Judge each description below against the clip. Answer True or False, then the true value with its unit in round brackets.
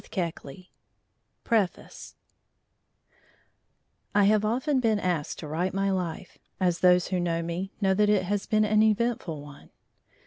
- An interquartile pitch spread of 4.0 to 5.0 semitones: False (3.3 semitones)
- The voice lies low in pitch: False (190 Hz)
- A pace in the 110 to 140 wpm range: True (135 wpm)